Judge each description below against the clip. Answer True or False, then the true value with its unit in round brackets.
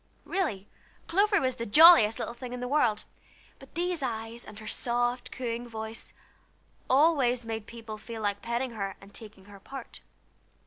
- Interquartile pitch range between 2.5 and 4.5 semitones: True (3.0 semitones)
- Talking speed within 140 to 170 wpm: True (165 wpm)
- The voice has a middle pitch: False (235 Hz)